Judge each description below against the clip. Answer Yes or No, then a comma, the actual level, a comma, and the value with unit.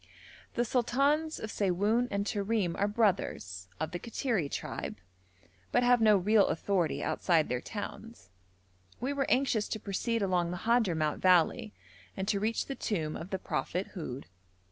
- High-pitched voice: Yes, high, 205 Hz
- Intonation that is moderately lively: Yes, average, 4.7 semitones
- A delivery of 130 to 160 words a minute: Yes, average, 155 wpm